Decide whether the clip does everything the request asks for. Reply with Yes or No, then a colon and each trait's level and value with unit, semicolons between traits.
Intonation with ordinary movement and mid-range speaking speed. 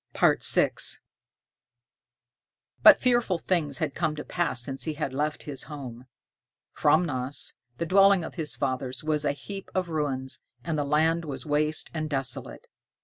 Yes: average, 3.4 semitones; average, 145 wpm